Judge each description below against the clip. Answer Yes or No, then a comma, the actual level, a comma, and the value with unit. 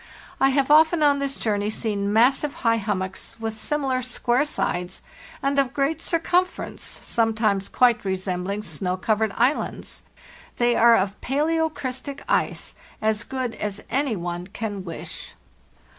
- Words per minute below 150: Yes, slow, 135 wpm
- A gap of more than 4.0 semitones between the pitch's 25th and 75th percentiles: Yes, average, 5.3 semitones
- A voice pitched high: Yes, high, 230 Hz